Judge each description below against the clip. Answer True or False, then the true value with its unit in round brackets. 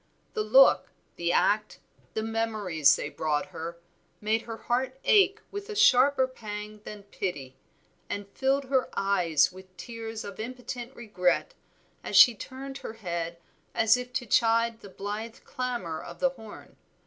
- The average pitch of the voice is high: True (225 Hz)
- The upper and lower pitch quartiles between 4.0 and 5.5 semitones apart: True (5.0 semitones)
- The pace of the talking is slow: False (150 wpm)